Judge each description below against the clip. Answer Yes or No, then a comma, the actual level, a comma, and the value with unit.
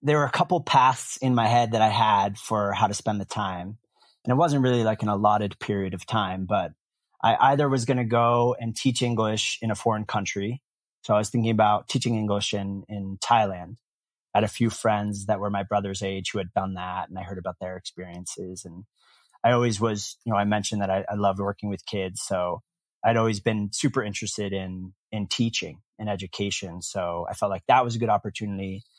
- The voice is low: Yes, low, 105 Hz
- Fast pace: Yes, fast, 215 wpm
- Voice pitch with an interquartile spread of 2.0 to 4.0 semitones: Yes, average, 2.9 semitones